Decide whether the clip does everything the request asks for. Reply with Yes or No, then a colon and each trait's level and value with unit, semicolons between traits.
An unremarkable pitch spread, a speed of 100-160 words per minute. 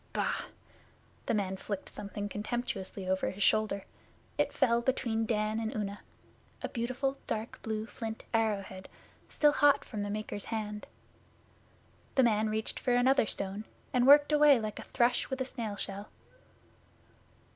Yes: average, 3.0 semitones; average, 150 wpm